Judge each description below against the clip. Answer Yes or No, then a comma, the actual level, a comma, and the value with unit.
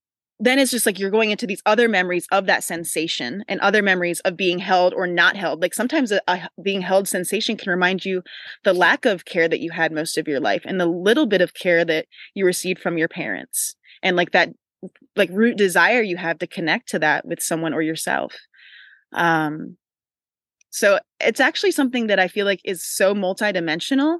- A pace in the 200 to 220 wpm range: Yes, fast, 205 wpm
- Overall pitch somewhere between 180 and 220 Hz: Yes, medium, 185 Hz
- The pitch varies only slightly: No, average, 3.6 semitones